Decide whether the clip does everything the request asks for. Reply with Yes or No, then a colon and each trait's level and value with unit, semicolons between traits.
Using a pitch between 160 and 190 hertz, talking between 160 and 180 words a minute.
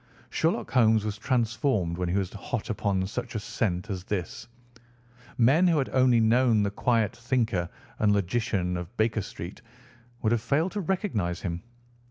No: low, 110 Hz; average, 165 wpm